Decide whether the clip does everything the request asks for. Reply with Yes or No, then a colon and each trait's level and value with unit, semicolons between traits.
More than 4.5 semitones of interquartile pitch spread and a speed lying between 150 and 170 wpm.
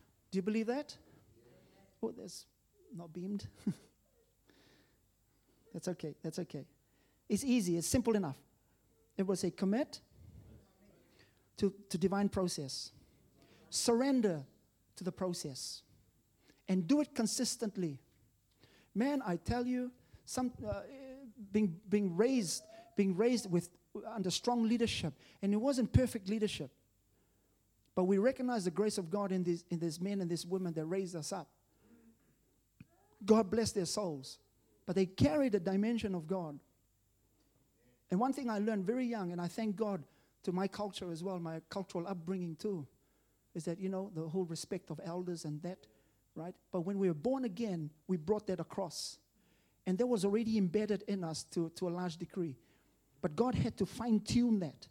Yes: average, 5.1 semitones; average, 155 wpm